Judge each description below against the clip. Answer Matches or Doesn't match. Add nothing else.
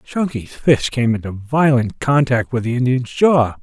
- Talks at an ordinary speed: Matches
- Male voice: Matches